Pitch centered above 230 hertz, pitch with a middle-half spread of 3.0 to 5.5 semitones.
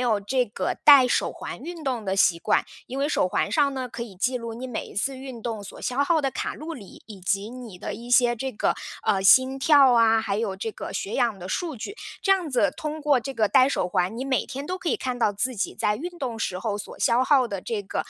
Yes: high, 245 Hz; average, 4.5 semitones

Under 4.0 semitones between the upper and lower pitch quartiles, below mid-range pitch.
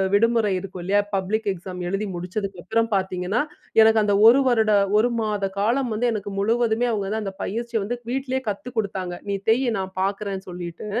No: average, 2.9 semitones; high, 210 Hz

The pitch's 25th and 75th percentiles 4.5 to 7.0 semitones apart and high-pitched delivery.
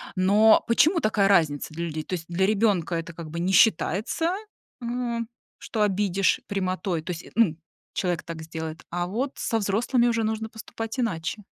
Yes: average, 4.9 semitones; high, 195 Hz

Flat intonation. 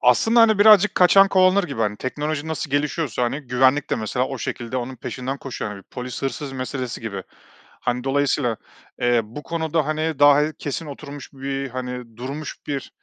No: average, 3.7 semitones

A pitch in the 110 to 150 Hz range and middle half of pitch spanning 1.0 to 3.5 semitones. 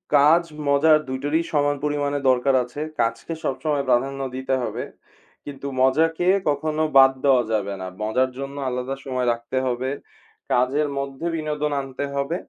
Yes: low, 135 Hz; narrow, 2.4 semitones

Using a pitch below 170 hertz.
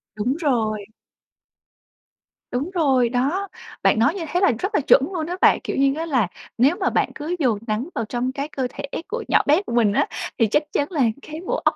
No: very high, 275 Hz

